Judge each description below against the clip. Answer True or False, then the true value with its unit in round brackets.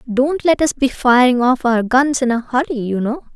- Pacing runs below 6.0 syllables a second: True (4.9 syllables/s)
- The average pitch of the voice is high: True (250 Hz)